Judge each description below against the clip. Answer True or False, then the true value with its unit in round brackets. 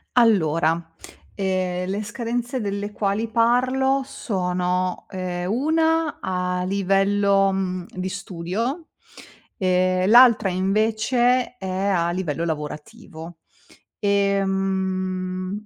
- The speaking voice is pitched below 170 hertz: False (195 Hz)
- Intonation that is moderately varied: True (3.8 semitones)